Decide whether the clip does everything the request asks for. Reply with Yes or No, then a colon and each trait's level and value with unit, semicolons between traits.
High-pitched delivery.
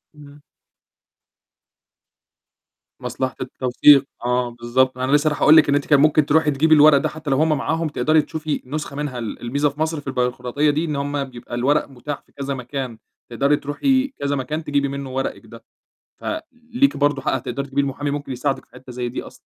No: medium, 140 Hz